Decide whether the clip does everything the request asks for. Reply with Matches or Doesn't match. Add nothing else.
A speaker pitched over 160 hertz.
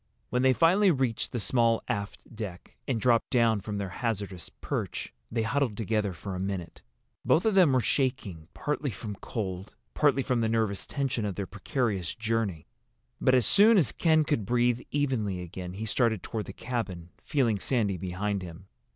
Doesn't match